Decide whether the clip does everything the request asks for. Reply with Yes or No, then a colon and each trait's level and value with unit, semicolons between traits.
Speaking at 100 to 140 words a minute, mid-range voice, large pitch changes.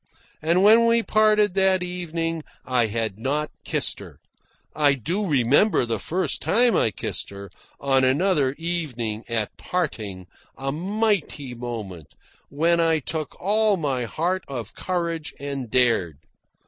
Yes: slow, 135 wpm; medium, 150 Hz; wide, 7.0 semitones